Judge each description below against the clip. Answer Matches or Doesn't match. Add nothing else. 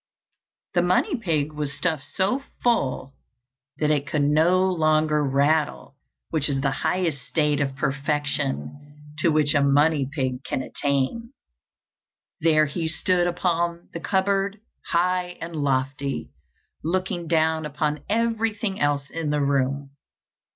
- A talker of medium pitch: Matches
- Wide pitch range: Doesn't match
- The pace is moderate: Doesn't match